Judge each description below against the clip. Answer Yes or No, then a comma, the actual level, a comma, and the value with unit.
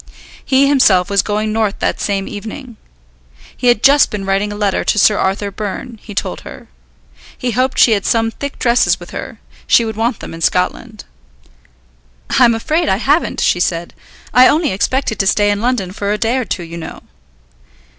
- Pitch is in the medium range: No, high, 215 Hz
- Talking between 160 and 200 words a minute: Yes, average, 195 wpm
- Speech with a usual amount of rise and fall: Yes, average, 3.9 semitones